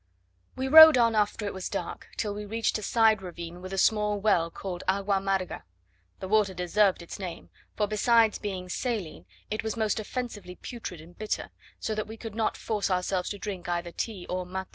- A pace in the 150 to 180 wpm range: No, average, 200 wpm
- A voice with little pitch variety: No, average, 3.1 semitones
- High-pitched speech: Yes, high, 205 Hz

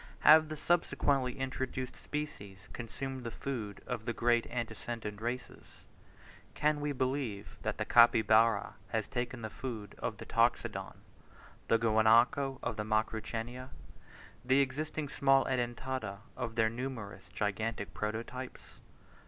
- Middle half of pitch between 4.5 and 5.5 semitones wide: No, average, 3.2 semitones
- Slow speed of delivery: Yes, slow, 125 wpm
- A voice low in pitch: Yes, low, 120 Hz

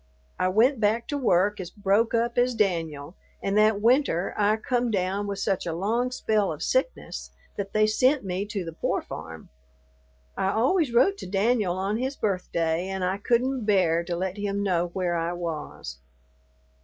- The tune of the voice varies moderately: Yes, average, 4.3 semitones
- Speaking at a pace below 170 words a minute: No, average, 180 wpm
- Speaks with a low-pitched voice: No, high, 200 Hz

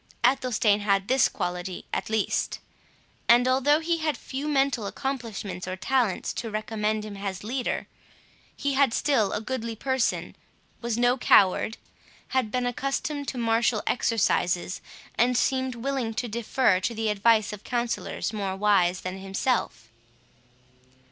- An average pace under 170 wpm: Yes, average, 140 wpm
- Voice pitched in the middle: No, high, 230 Hz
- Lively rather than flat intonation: No, average, 4.2 semitones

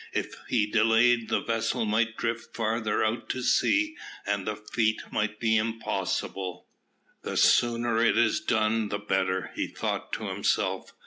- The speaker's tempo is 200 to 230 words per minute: No, average, 150 wpm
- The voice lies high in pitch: No, low, 110 Hz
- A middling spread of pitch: No, narrow, 1.5 semitones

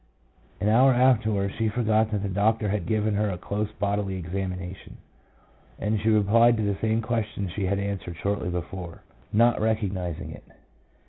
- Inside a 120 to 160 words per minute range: No, average, 175 wpm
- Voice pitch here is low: Yes, low, 105 Hz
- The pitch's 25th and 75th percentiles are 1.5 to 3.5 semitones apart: Yes, narrow, 2.4 semitones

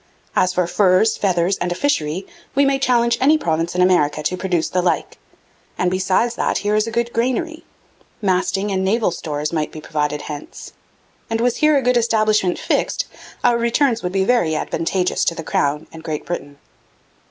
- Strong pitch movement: Yes, wide, 5.9 semitones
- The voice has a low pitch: No, high, 190 Hz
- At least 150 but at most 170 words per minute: No, average, 185 wpm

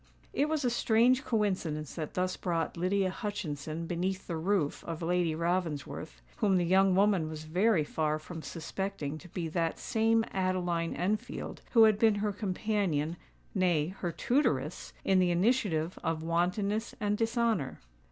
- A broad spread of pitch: No, average, 4.2 semitones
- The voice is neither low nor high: Yes, medium, 180 Hz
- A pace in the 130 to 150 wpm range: Yes, average, 145 wpm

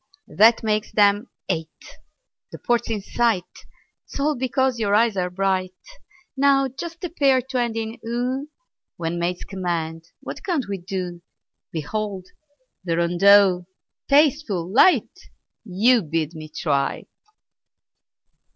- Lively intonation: Yes, wide, 5.9 semitones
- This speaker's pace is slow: Yes, slow, 125 wpm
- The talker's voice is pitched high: Yes, high, 205 Hz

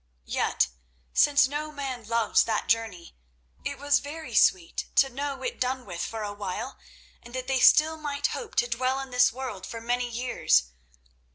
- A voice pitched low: No, very high, 250 Hz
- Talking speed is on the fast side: No, average, 175 wpm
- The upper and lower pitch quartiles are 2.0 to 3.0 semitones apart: No, average, 3.4 semitones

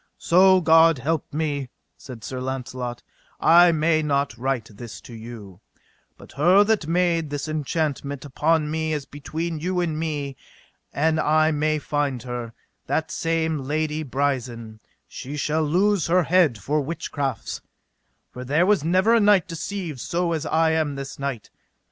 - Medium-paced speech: Yes, average, 150 wpm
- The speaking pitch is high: No, medium, 155 Hz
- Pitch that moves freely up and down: No, average, 3.3 semitones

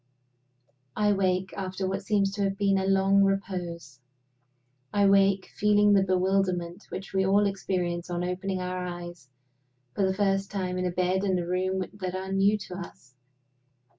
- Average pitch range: No, narrow, 1.3 semitones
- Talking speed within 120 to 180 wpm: Yes, average, 165 wpm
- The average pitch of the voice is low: No, high, 190 Hz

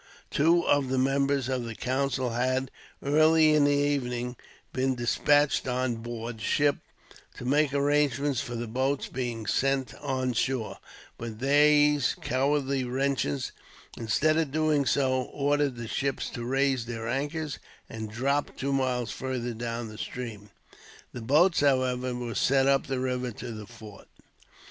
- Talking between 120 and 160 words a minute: Yes, average, 150 wpm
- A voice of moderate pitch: No, low, 130 Hz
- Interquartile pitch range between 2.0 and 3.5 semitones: Yes, average, 2.8 semitones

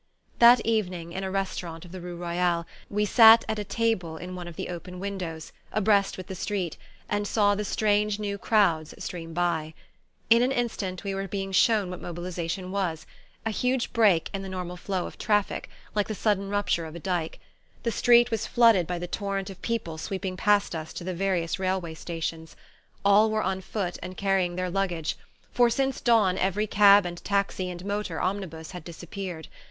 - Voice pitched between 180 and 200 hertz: Yes, high, 190 Hz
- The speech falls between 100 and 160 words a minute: No, average, 190 wpm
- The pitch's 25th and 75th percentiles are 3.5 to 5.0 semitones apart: No, average, 3.0 semitones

